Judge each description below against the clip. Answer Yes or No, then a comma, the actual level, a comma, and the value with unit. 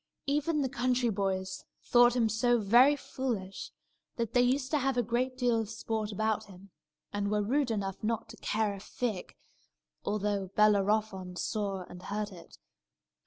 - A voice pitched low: No, high, 220 Hz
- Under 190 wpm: Yes, average, 165 wpm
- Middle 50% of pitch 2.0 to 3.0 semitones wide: No, average, 3.5 semitones